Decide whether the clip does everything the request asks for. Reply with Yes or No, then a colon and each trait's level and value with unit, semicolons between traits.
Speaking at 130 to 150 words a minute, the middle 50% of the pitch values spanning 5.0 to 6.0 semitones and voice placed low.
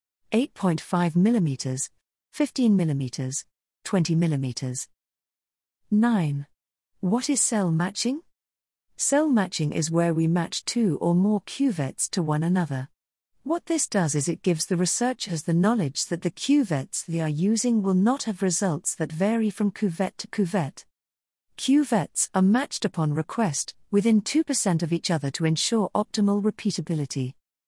No: average, 140 wpm; wide, 5.4 semitones; medium, 185 Hz